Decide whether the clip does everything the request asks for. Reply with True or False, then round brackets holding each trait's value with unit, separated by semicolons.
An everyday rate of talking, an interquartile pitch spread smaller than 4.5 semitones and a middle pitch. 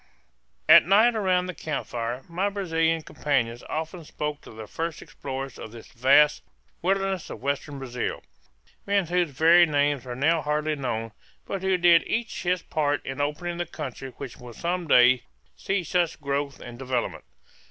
False (165 wpm; 4.8 semitones; 150 Hz)